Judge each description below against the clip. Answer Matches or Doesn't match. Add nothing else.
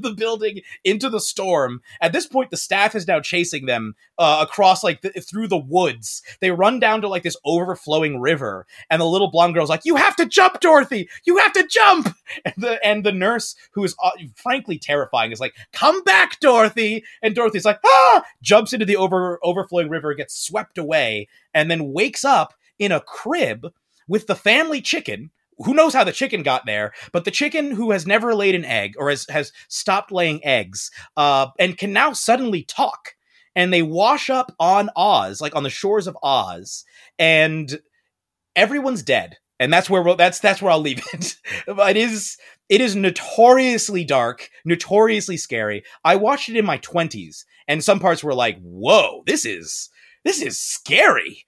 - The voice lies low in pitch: Doesn't match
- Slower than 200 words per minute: Matches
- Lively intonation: Matches